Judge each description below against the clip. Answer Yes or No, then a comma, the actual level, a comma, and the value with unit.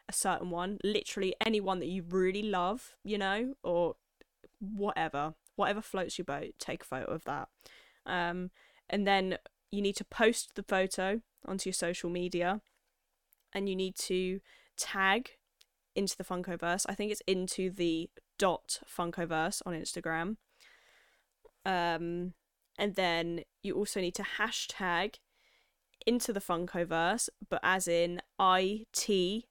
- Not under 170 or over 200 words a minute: No, average, 140 wpm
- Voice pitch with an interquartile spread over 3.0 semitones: No, narrow, 2.5 semitones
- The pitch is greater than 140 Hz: Yes, high, 190 Hz